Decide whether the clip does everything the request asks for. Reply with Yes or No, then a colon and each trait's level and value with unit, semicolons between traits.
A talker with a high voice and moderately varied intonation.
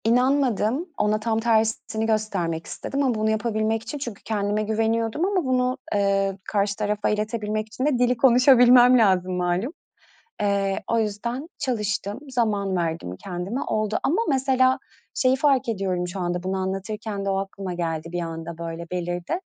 Yes: high, 215 Hz; average, 4.1 semitones